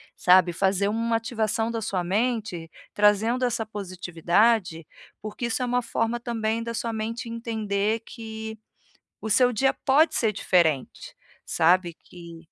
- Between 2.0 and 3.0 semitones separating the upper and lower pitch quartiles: No, average, 3.7 semitones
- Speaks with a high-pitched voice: Yes, high, 220 Hz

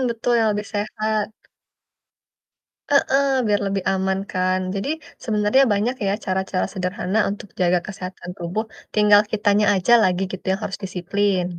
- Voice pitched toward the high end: Yes, high, 200 Hz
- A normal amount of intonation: No, narrow, 2.3 semitones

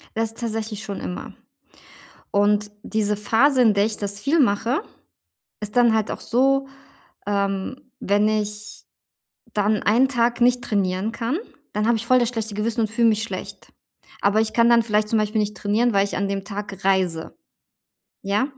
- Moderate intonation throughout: No, narrow, 2.3 semitones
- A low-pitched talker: No, high, 215 Hz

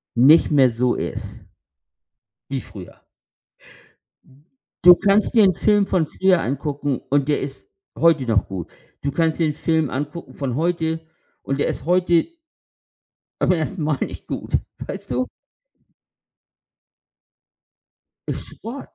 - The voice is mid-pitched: Yes, medium, 155 Hz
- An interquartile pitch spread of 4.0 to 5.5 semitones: Yes, average, 4.3 semitones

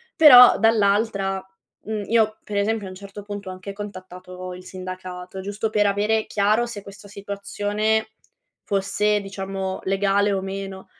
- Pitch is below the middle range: No, high, 200 Hz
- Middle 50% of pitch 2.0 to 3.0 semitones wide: No, narrow, 1.6 semitones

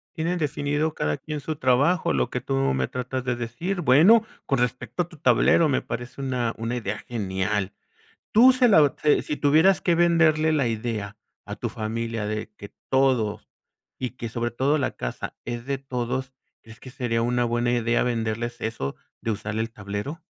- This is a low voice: Yes, low, 125 Hz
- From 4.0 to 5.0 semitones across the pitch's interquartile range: Yes, average, 4.5 semitones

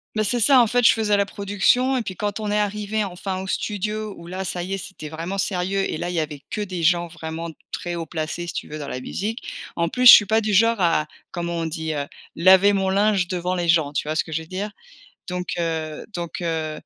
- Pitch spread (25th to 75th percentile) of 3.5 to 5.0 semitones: Yes, average, 3.8 semitones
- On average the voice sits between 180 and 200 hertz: Yes, medium, 185 Hz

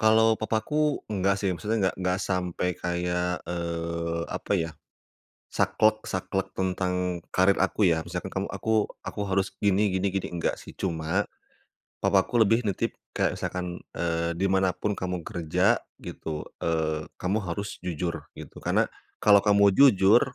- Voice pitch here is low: Yes, very low, 95 Hz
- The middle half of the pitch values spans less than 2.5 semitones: No, average, 2.8 semitones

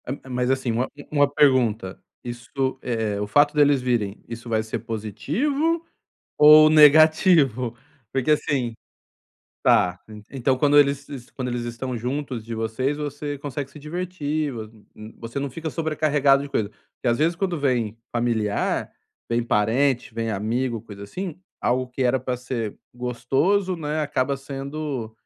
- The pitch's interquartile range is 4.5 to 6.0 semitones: No, average, 4.1 semitones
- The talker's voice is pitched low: Yes, low, 130 Hz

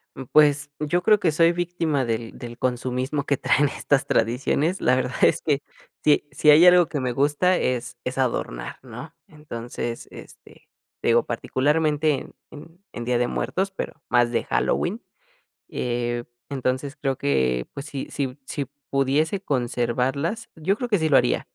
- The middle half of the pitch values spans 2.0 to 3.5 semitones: No, average, 4.2 semitones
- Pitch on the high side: No, medium, 140 Hz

